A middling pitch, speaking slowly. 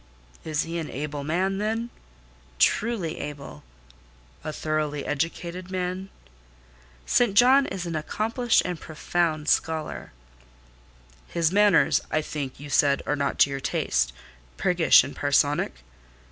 Yes: medium, 160 Hz; slow, 120 wpm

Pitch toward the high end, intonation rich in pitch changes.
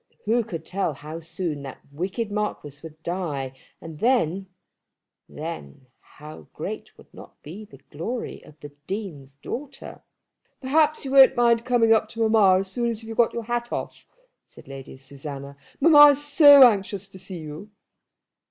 Yes: high, 195 Hz; wide, 7.6 semitones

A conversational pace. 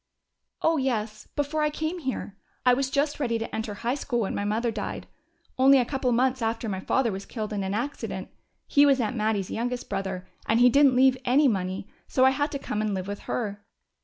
No: fast, 220 wpm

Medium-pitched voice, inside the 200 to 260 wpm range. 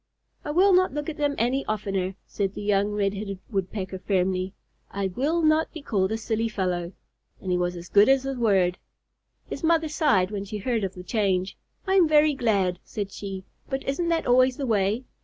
No: high, 210 Hz; fast, 205 wpm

